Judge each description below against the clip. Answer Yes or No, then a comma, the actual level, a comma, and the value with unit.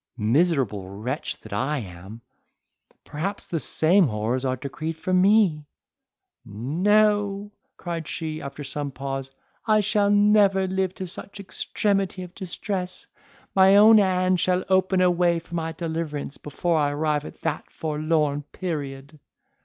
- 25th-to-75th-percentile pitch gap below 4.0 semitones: No, average, 4.9 semitones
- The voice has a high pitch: No, medium, 165 Hz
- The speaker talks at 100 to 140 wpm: Yes, slow, 135 wpm